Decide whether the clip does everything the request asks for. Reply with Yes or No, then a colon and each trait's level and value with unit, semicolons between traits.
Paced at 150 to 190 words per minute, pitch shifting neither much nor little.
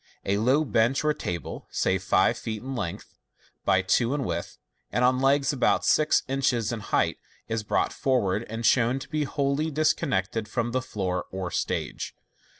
Yes: average, 170 wpm; average, 4.4 semitones